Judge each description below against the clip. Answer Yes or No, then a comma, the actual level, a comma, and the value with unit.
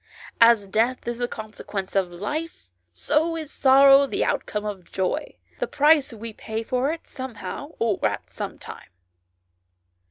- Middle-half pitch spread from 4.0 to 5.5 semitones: Yes, average, 5.0 semitones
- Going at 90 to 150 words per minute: Yes, average, 140 wpm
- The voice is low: No, high, 235 Hz